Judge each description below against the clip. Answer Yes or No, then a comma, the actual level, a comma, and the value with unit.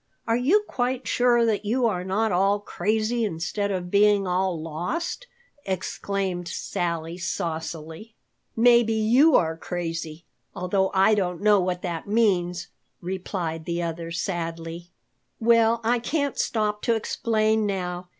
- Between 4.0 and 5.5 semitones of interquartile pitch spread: Yes, average, 4.3 semitones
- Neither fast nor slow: No, slow, 130 wpm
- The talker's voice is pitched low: No, high, 195 Hz